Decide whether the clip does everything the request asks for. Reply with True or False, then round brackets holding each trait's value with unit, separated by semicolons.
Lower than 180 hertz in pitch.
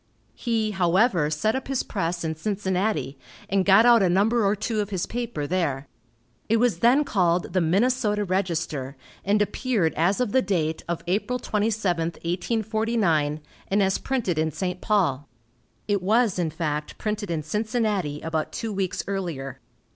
False (195 Hz)